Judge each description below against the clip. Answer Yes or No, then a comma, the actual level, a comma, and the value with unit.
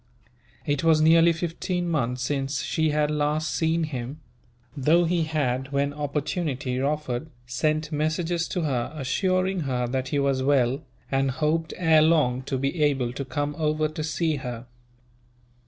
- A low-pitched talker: No, medium, 150 Hz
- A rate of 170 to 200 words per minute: No, average, 155 wpm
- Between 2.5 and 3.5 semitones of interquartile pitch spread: Yes, average, 3.0 semitones